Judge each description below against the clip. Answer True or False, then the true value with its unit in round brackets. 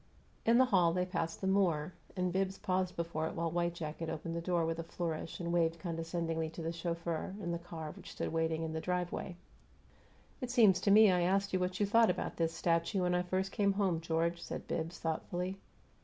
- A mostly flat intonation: True (2.1 semitones)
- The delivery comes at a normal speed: False (215 wpm)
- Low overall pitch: False (175 Hz)